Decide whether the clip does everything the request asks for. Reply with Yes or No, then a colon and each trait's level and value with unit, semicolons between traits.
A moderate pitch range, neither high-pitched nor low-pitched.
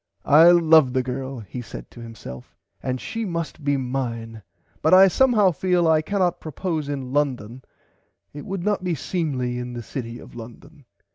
No: wide, 5.7 semitones; medium, 145 Hz